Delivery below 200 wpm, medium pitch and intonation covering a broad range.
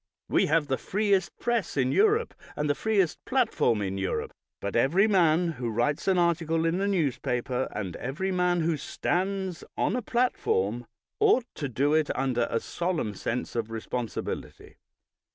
Yes: average, 160 wpm; medium, 160 Hz; wide, 7.5 semitones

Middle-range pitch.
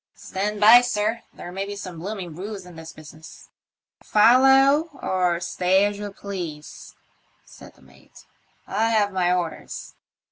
No: high, 195 Hz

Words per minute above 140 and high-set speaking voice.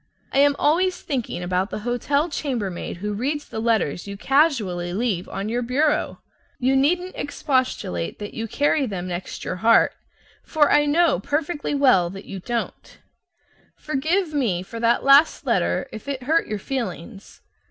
Yes: average, 160 wpm; high, 245 Hz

